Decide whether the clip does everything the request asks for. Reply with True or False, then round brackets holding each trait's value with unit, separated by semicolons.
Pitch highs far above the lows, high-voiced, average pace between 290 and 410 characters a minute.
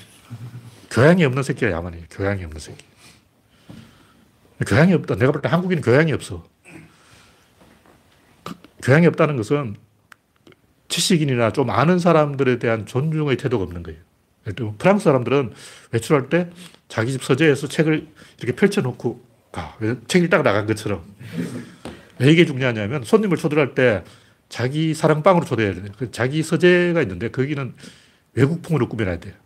False (6.1 semitones; 130 Hz; 320 characters per minute)